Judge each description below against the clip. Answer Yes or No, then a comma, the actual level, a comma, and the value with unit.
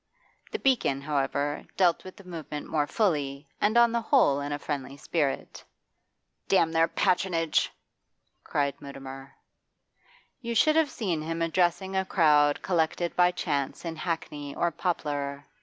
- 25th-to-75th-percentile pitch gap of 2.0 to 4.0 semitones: No, average, 4.4 semitones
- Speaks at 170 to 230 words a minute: No, average, 140 wpm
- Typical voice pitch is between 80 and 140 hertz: No, medium, 165 Hz